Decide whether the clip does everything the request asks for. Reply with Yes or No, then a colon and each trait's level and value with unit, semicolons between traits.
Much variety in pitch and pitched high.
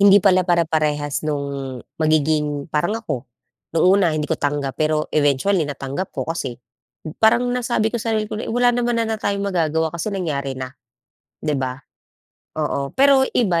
No: wide, 5.7 semitones; medium, 160 Hz